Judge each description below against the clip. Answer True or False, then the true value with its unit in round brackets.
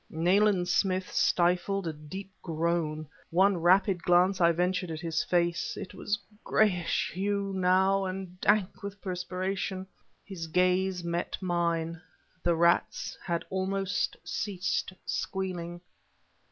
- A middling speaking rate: False (125 wpm)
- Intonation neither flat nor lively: False (2.0 semitones)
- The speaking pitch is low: False (180 Hz)